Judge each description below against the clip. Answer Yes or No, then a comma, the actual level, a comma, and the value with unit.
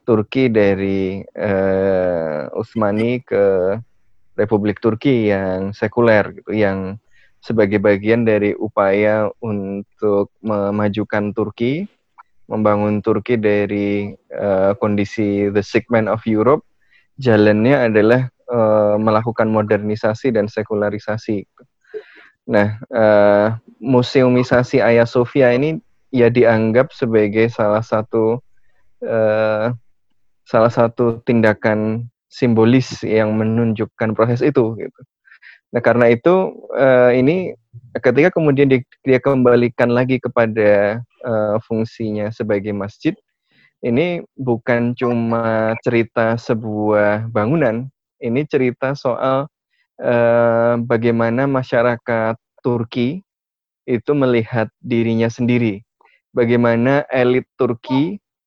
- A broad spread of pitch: No, narrow, 2.6 semitones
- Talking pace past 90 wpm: No, slow, 85 wpm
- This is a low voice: Yes, low, 115 Hz